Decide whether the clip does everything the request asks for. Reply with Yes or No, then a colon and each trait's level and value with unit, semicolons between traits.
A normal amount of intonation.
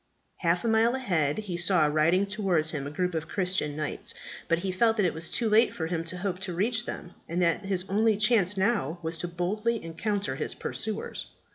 Yes: average, 4.1 semitones